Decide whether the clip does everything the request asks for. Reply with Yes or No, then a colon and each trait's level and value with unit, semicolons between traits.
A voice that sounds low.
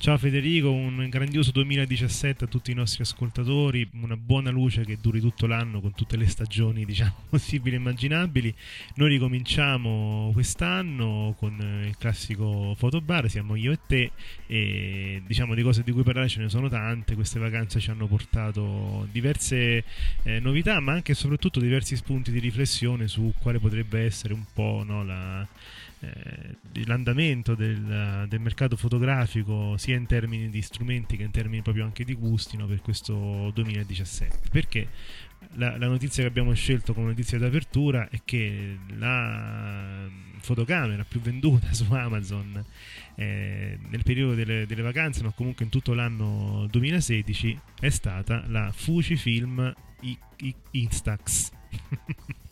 Yes: low, 115 Hz